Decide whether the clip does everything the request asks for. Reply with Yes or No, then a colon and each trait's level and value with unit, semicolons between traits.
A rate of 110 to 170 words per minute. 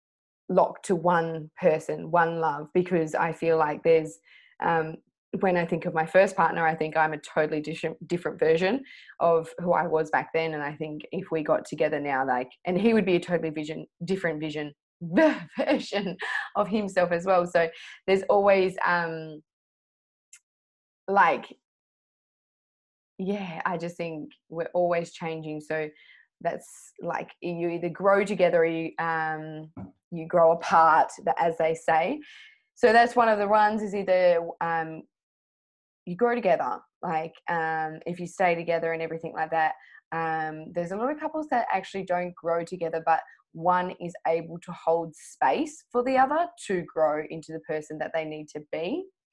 Yes: average, 165 wpm